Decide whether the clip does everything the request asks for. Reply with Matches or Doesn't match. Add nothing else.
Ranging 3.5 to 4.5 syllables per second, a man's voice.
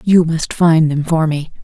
Doesn't match